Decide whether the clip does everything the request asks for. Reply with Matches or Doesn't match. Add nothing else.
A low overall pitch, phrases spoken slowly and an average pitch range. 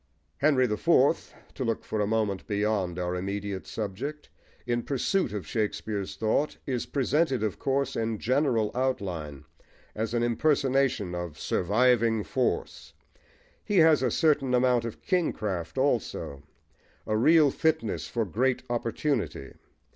Matches